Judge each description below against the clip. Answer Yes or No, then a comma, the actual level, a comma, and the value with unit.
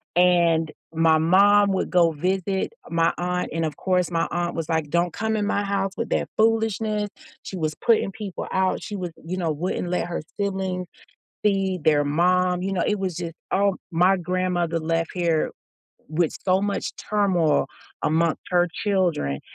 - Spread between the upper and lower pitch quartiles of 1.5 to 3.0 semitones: Yes, average, 2.7 semitones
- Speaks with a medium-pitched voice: Yes, medium, 180 Hz